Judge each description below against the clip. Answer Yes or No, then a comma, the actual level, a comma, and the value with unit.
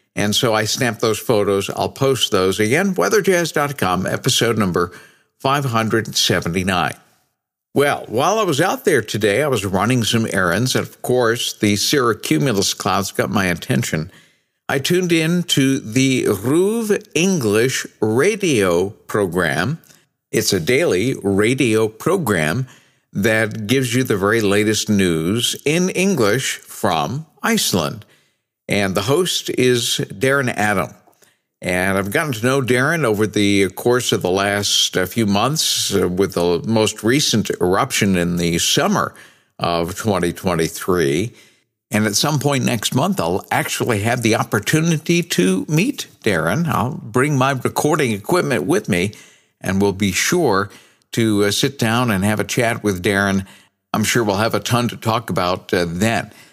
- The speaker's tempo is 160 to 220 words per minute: No, average, 140 wpm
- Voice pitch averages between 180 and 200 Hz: No, low, 115 Hz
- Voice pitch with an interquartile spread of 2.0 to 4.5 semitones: No, wide, 5.4 semitones